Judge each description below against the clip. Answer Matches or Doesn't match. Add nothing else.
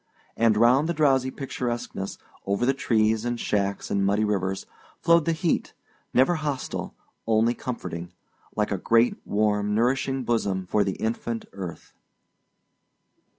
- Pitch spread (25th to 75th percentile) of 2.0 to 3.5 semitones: Doesn't match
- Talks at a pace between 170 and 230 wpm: Doesn't match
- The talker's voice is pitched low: Matches